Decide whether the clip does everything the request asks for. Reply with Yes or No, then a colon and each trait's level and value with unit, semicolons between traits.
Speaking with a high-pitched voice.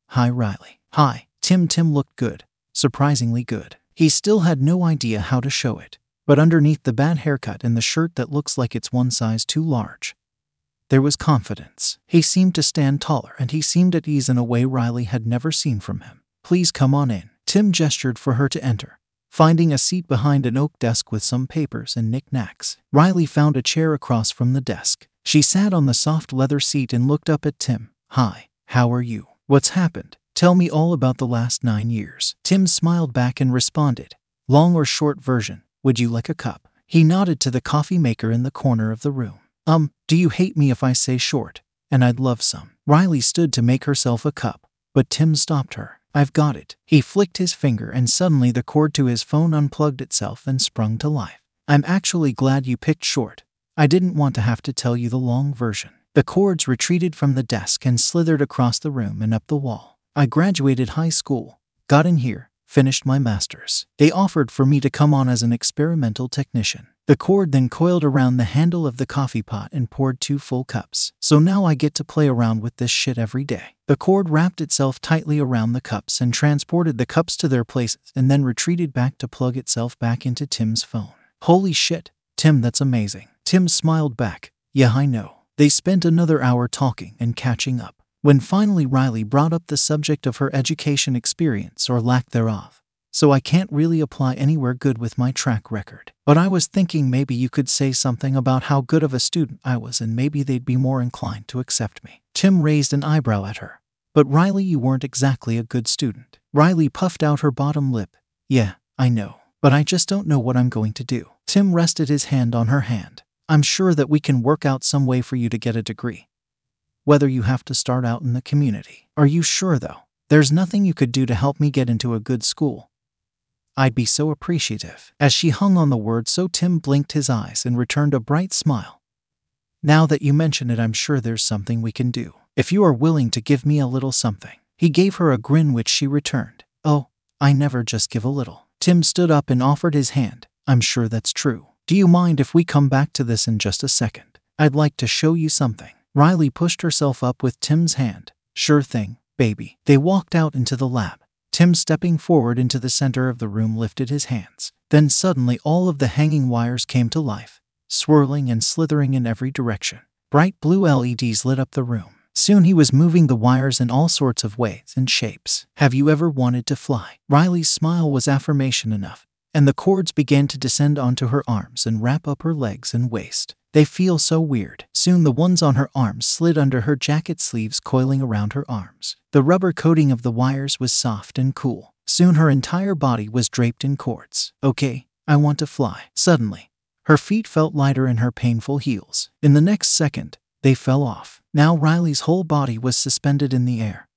No: low, 135 Hz